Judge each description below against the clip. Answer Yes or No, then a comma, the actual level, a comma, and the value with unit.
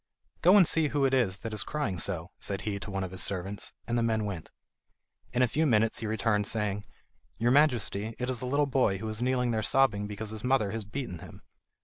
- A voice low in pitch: Yes, low, 110 Hz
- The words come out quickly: Yes, fast, 235 wpm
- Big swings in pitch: No, average, 4.0 semitones